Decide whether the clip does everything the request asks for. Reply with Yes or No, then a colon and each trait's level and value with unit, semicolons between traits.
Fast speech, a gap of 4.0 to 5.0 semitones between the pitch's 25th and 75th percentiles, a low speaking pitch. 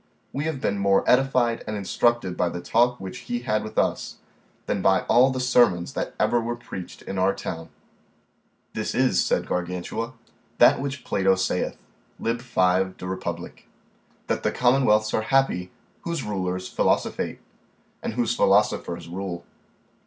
No: average, 155 wpm; average, 4.7 semitones; low, 105 Hz